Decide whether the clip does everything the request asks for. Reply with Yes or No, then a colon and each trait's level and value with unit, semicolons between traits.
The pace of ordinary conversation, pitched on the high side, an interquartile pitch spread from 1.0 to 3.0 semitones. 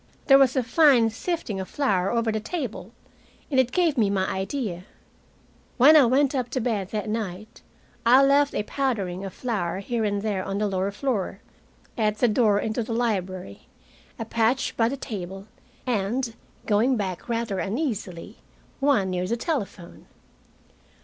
No: average, 165 wpm; high, 225 Hz; average, 4.7 semitones